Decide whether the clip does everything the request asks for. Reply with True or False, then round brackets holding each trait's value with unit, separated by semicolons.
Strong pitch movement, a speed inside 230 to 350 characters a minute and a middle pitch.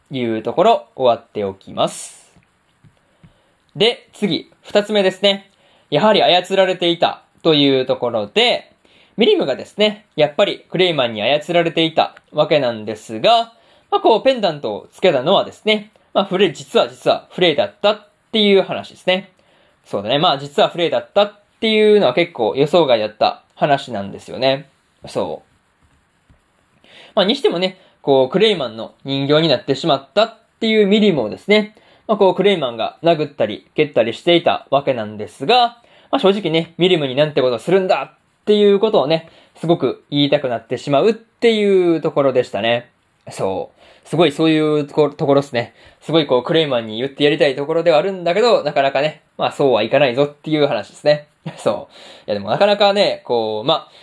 False (6.4 semitones; 380 characters per minute; 165 Hz)